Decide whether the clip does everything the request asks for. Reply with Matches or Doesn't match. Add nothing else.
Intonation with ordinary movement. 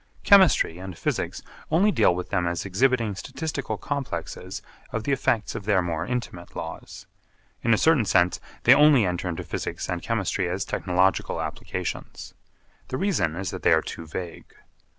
Doesn't match